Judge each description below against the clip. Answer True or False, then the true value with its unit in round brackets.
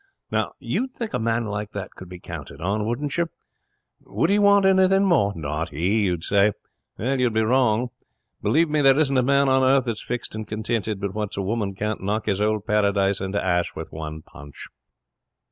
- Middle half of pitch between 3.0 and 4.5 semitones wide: False (5.2 semitones)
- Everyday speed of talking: True (195 wpm)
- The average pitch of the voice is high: False (110 Hz)